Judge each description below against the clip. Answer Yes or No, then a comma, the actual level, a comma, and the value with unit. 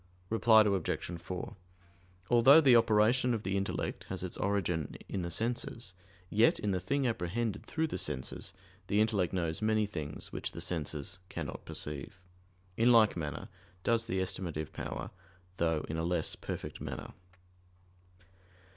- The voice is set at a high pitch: No, very low, 95 Hz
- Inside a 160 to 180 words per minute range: No, average, 145 wpm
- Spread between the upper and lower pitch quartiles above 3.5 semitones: Yes, average, 5.0 semitones